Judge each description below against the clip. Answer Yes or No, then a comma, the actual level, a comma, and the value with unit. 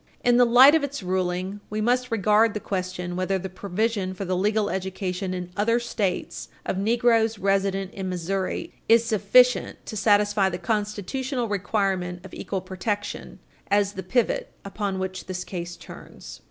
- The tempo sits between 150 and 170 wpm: Yes, average, 160 wpm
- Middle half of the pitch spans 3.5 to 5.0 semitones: No, average, 3.0 semitones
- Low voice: No, high, 200 Hz